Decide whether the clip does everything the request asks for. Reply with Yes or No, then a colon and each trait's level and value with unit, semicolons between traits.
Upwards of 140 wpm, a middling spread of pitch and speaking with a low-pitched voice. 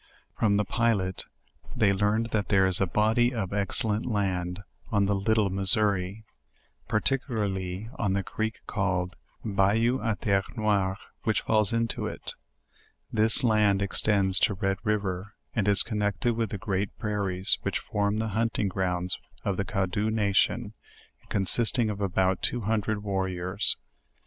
No: average, 150 wpm; narrow, 2.3 semitones; low, 100 Hz